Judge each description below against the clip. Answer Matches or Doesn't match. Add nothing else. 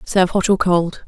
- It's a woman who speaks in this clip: Matches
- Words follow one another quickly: Matches